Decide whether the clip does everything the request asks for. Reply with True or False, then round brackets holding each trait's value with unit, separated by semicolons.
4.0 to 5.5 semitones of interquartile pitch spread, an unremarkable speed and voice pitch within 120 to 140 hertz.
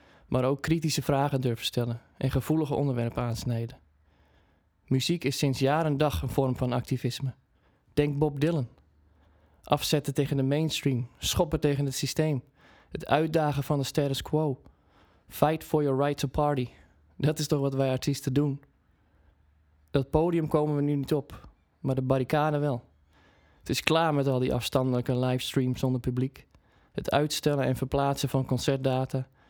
False (3.5 semitones; 155 wpm; 135 Hz)